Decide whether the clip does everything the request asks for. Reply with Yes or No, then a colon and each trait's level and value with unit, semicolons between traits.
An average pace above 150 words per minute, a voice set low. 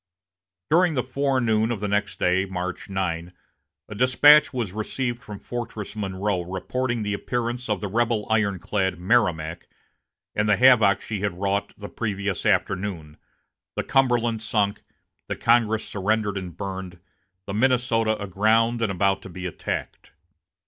No: average, 140 wpm; low, 105 Hz